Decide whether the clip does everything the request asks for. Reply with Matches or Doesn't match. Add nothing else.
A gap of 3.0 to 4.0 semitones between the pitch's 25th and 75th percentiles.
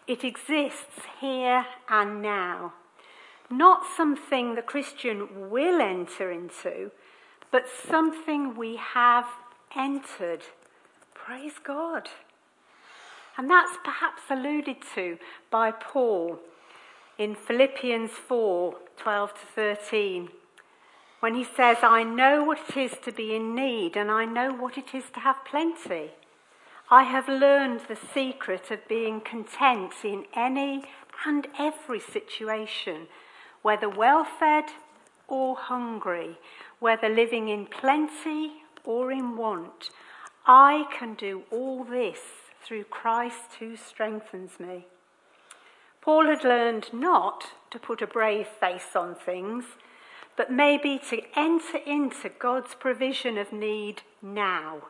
Doesn't match